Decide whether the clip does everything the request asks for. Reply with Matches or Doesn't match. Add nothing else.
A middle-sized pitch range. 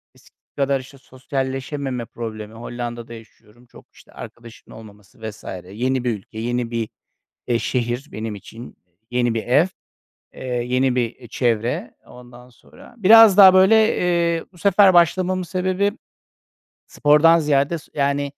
Doesn't match